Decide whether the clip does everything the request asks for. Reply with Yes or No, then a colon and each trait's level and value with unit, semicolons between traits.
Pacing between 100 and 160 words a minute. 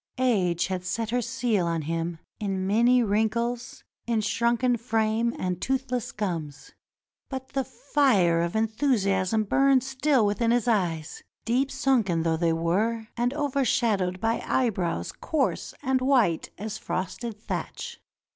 Yes: slow, 135 wpm